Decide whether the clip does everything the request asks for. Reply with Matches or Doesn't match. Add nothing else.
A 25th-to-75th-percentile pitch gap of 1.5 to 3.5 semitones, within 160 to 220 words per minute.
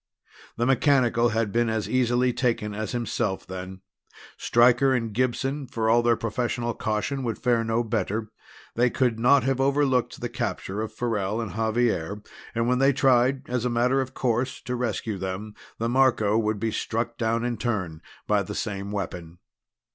Matches